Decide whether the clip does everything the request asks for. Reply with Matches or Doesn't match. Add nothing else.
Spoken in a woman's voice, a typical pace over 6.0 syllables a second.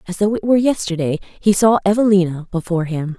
Matches